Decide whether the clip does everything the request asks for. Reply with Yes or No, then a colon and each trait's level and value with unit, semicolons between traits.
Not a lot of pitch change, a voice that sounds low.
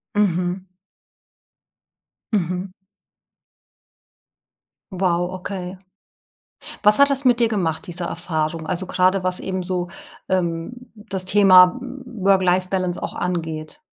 No: narrow, 1.9 semitones; medium, 185 Hz